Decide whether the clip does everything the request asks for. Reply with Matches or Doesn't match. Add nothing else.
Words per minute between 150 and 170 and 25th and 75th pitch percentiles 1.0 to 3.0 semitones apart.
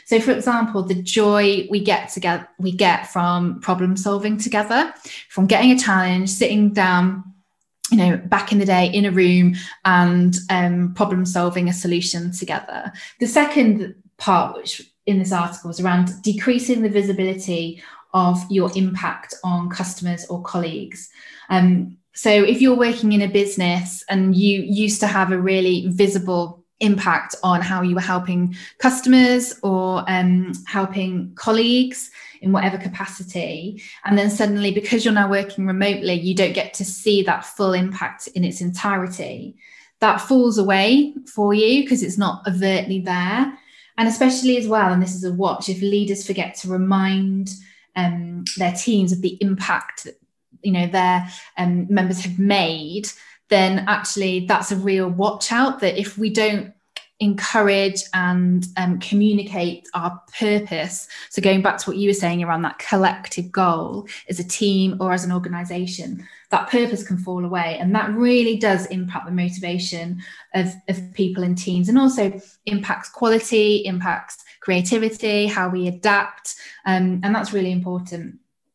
Matches